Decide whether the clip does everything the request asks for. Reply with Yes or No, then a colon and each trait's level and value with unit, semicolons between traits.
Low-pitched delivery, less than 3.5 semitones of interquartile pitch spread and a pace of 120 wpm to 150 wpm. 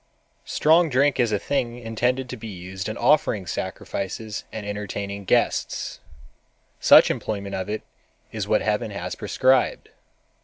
No: low, 110 Hz; average, 4.2 semitones; average, 140 wpm